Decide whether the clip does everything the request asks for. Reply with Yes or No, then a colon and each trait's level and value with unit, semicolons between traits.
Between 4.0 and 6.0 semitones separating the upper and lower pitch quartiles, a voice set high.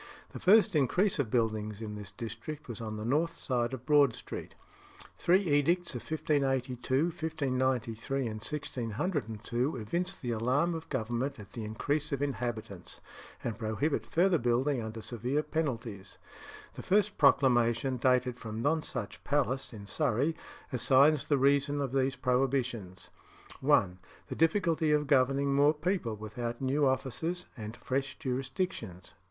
No: average, 4.4 semitones; low, 130 Hz